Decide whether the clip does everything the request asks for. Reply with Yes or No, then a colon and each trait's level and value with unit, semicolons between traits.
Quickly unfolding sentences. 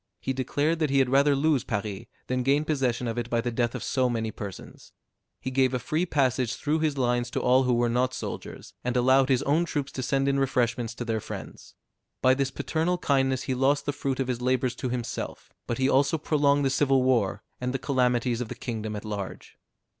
Yes: fast, 220 wpm